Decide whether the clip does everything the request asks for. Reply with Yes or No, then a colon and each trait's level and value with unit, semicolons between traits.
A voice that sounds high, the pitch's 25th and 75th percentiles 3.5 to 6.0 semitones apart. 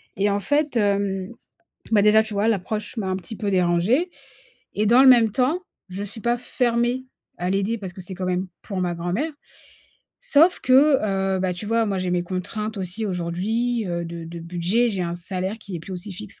Yes: high, 200 Hz; average, 4.1 semitones